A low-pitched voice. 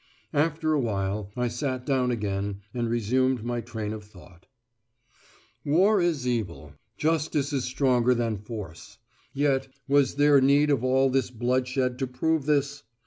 Yes: low, 130 Hz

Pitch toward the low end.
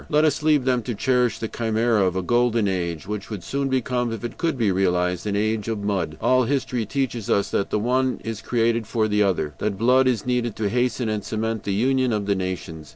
Yes: low, 115 Hz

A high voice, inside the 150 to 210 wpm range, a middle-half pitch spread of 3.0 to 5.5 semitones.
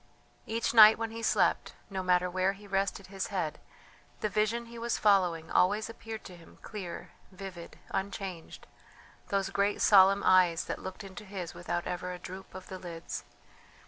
No: high, 195 Hz; average, 170 wpm; narrow, 2.5 semitones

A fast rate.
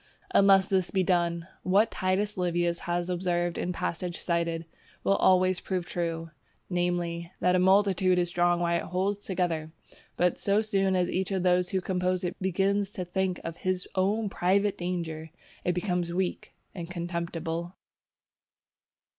No: average, 155 wpm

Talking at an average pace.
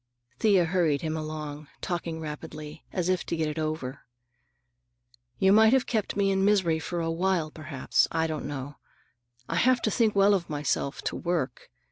Yes: average, 175 wpm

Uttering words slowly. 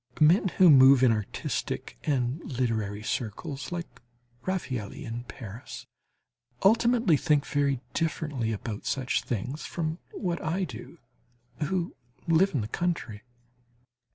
Yes: slow, 120 wpm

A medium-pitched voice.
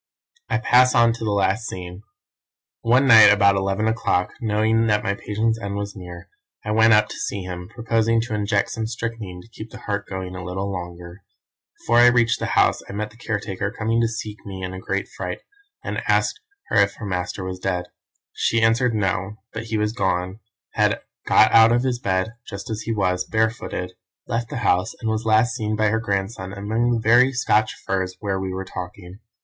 No: low, 105 Hz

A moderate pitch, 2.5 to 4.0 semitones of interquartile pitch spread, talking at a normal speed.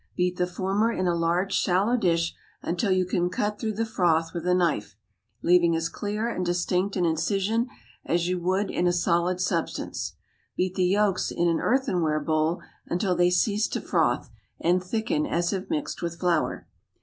Yes: medium, 180 Hz; average, 2.8 semitones; average, 180 wpm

